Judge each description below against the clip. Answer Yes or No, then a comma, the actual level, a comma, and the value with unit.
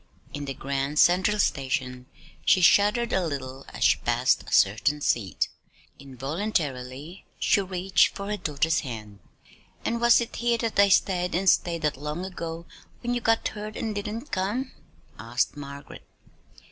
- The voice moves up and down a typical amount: No, wide, 7.1 semitones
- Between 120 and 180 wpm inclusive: Yes, average, 160 wpm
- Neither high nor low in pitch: Yes, medium, 170 Hz